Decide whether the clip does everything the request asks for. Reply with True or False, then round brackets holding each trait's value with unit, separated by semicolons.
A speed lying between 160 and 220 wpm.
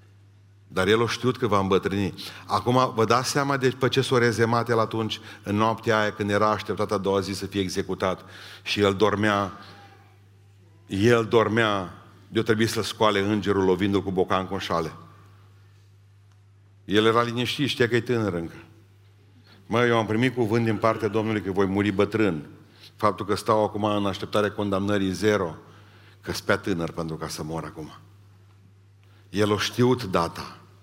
True (170 wpm)